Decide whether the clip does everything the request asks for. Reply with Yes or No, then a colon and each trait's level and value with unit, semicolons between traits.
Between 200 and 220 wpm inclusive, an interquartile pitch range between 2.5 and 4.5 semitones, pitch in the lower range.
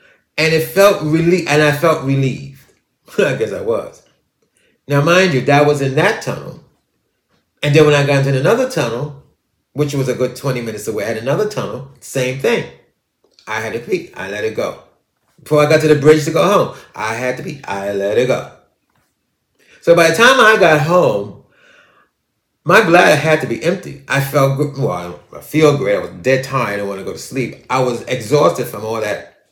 No: fast, 205 wpm; average, 4.0 semitones; medium, 145 Hz